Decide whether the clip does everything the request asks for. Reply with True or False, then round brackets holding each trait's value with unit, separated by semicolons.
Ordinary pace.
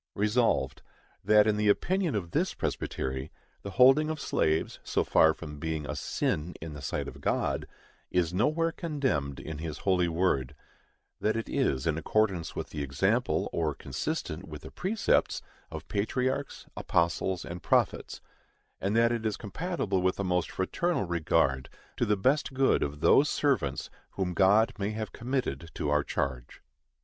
True (160 wpm)